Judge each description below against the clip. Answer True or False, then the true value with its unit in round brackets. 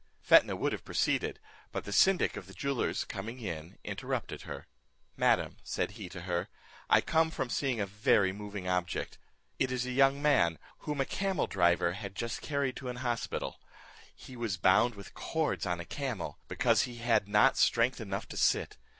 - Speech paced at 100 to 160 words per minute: False (185 wpm)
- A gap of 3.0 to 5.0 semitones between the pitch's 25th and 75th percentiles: False (5.5 semitones)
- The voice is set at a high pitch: False (115 Hz)